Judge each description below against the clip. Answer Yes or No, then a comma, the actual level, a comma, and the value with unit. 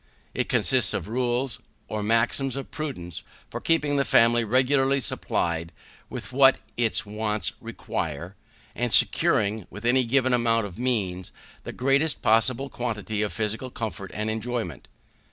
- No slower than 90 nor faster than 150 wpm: Yes, average, 140 wpm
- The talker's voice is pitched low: Yes, low, 115 Hz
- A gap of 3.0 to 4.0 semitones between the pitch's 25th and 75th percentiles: Yes, average, 3.6 semitones